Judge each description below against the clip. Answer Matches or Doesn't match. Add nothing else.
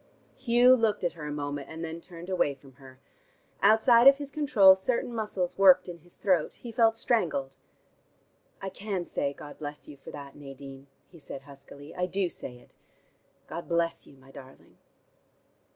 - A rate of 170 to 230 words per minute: Matches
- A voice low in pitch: Doesn't match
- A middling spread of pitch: Doesn't match